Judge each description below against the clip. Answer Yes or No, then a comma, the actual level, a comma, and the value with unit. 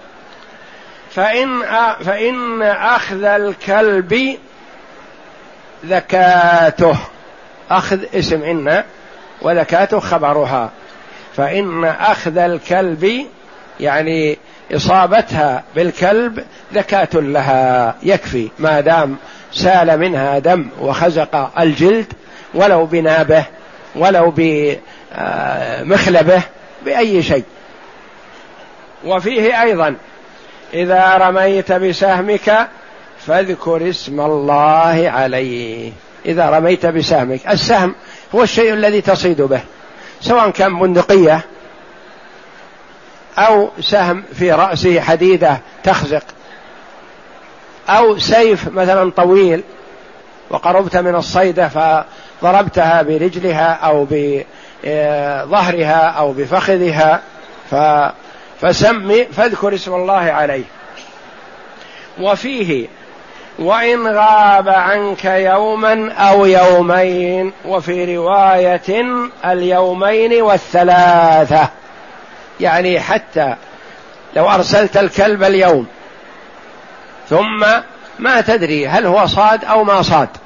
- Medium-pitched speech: Yes, medium, 180 Hz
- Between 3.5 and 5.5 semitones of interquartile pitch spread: Yes, average, 4.0 semitones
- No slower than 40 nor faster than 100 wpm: Yes, average, 75 wpm